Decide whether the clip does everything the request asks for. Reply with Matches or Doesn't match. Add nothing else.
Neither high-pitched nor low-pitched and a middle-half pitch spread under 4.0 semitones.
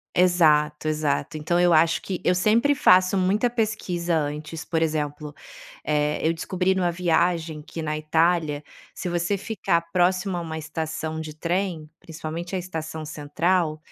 Matches